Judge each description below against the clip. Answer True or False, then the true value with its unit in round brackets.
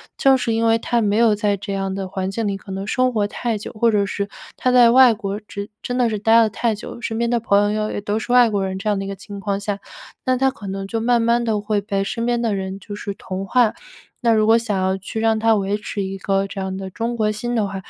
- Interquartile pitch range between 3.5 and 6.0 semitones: False (2.7 semitones)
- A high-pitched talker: True (210 Hz)